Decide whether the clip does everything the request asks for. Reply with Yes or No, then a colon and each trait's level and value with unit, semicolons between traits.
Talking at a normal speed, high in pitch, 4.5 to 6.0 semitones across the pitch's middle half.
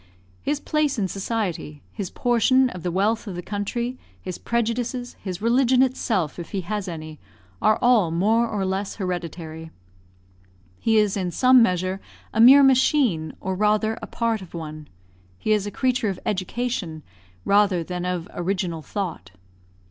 Yes: average, 155 wpm; high, 200 Hz; average, 4.8 semitones